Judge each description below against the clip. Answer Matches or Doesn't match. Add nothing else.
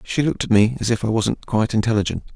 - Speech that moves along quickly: Matches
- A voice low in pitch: Matches